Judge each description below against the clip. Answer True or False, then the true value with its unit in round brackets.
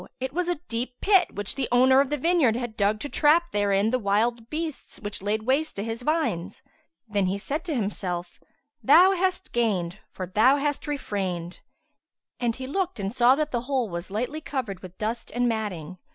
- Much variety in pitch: True (6.1 semitones)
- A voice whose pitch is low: False (240 Hz)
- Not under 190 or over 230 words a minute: True (195 wpm)